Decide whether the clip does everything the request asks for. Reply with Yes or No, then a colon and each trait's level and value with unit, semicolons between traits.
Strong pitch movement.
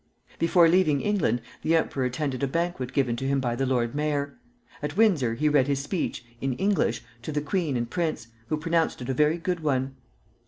No: average, 4.4 semitones